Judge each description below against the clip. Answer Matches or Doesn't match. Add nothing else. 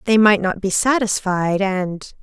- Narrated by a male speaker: Doesn't match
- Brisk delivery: Doesn't match